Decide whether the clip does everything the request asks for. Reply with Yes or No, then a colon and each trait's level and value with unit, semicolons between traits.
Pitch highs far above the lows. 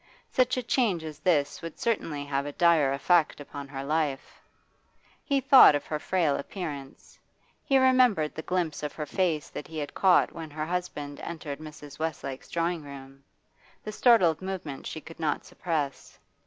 No: average, 3.8 semitones